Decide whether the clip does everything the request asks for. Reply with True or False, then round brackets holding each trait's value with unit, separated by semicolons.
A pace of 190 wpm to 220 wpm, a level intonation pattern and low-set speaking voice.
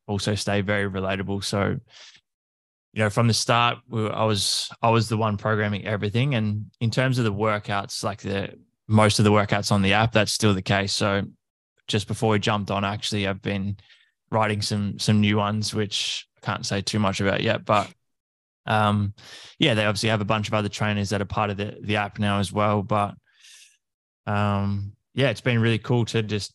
True (205 wpm; 1.6 semitones; 105 Hz)